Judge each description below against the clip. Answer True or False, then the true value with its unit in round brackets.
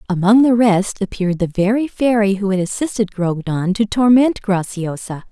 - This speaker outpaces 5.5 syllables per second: False (4.9 syllables/s)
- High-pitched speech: True (205 Hz)